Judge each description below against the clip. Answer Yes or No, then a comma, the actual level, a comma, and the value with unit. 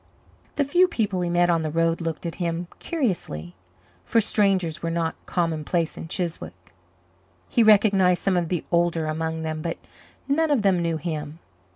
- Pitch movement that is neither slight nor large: Yes, average, 3.3 semitones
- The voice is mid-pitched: Yes, medium, 170 Hz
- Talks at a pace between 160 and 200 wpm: Yes, average, 170 wpm